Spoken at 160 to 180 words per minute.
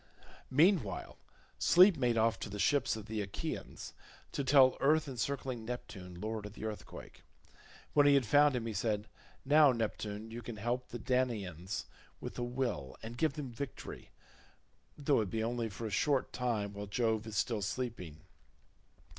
Yes: average, 165 wpm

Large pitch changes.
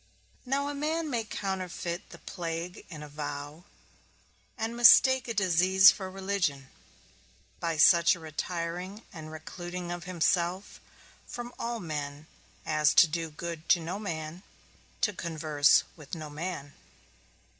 No: average, 3.7 semitones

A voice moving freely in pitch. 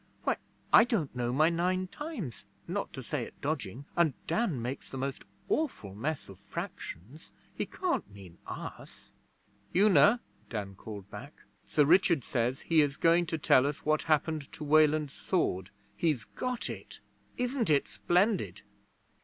Yes: wide, 6.7 semitones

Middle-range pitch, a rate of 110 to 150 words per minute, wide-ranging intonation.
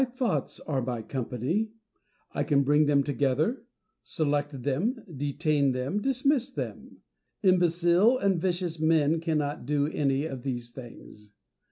No: medium, 150 Hz; average, 140 wpm; average, 5.0 semitones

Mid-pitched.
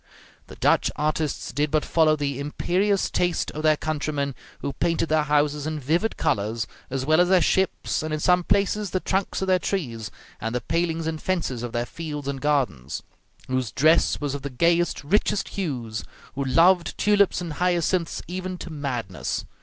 Yes: medium, 155 Hz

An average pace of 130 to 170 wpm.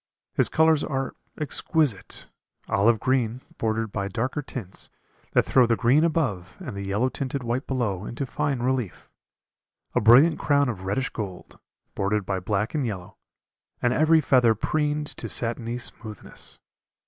Yes: average, 150 wpm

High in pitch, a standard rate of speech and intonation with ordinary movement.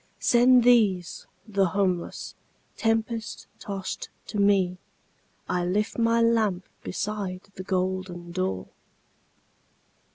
No: high, 195 Hz; slow, 90 wpm; average, 3.4 semitones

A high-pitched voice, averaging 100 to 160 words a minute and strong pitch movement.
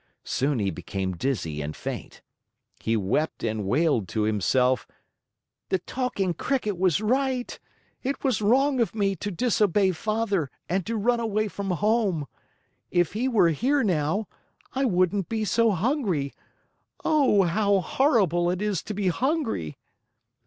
Yes: high, 195 Hz; average, 145 wpm; wide, 6.8 semitones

